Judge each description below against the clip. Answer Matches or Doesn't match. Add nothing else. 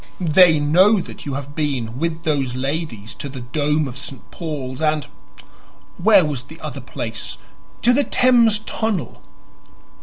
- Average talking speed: Matches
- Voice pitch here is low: Doesn't match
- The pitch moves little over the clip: Doesn't match